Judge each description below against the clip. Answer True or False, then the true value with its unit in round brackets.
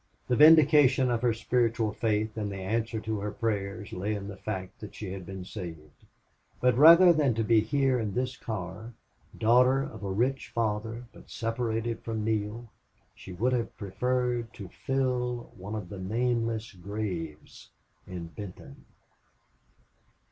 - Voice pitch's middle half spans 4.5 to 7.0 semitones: False (3.4 semitones)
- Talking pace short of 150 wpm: False (155 wpm)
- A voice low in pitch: True (110 Hz)